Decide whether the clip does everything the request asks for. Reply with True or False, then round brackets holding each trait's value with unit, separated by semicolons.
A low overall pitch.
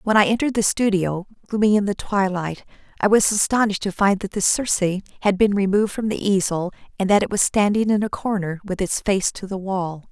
False (200 Hz)